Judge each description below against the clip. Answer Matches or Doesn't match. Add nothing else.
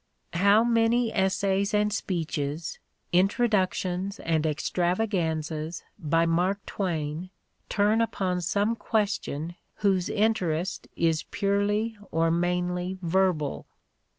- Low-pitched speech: Doesn't match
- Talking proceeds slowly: Matches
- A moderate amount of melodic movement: Matches